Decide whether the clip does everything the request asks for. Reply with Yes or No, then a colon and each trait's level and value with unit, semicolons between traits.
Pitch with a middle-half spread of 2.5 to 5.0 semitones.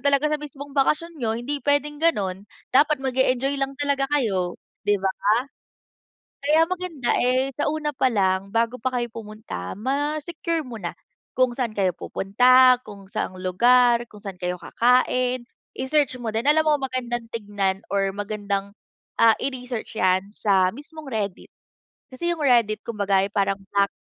No: wide, 5.5 semitones